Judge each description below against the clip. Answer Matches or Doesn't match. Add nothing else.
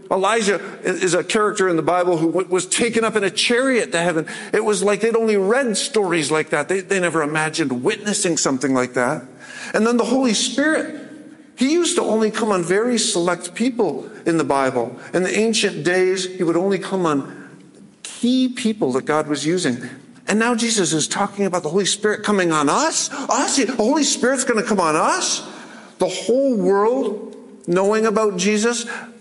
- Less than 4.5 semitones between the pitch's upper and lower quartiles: Doesn't match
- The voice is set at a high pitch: Matches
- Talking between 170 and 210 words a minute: Matches